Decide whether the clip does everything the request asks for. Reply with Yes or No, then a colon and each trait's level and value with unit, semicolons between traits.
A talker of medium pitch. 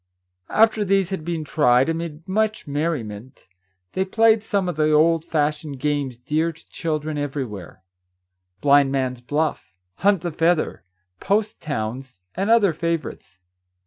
Yes: medium, 155 Hz